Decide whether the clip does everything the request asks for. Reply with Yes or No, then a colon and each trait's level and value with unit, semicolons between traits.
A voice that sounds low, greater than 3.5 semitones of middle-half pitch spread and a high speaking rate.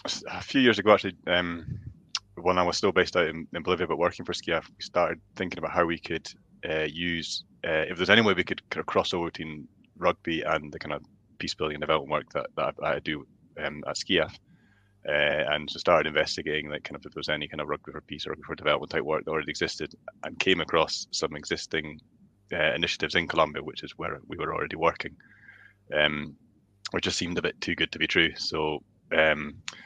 Yes: very low, 85 Hz; average, 3.9 semitones; fast, 225 wpm